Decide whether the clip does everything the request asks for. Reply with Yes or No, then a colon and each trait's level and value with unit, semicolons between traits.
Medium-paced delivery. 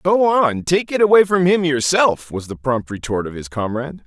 No: fast, 220 wpm